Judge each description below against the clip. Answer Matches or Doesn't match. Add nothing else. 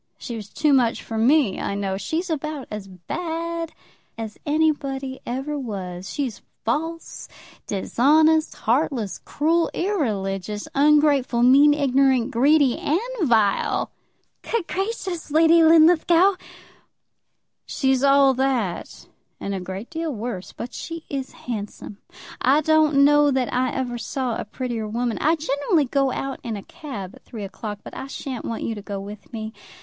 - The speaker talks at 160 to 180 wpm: Doesn't match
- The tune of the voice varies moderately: Doesn't match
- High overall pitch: Matches